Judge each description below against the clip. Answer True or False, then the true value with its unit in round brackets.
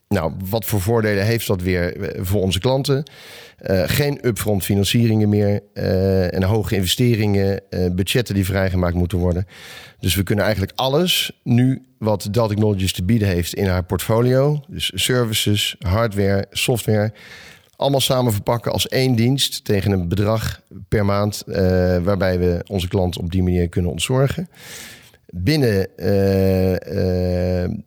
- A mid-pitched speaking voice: False (100 Hz)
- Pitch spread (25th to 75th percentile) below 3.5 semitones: False (3.8 semitones)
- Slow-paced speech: False (145 wpm)